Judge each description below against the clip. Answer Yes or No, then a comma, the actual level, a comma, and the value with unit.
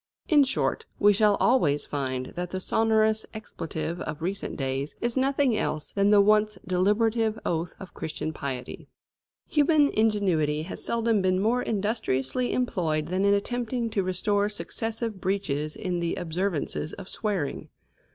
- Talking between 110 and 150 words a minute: Yes, average, 145 wpm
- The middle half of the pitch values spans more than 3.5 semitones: Yes, average, 5.2 semitones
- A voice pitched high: Yes, high, 200 Hz